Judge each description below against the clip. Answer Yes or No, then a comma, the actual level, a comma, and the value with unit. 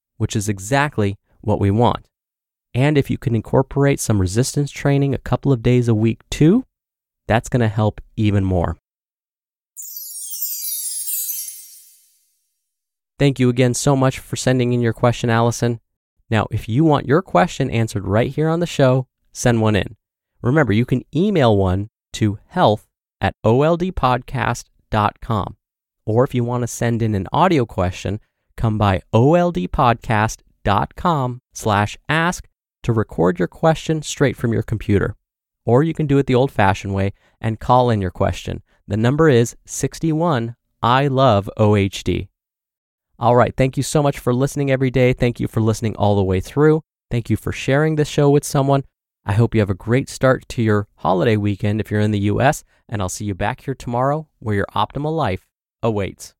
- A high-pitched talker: No, low, 115 Hz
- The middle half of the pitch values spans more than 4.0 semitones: Yes, average, 4.6 semitones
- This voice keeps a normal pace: Yes, average, 170 wpm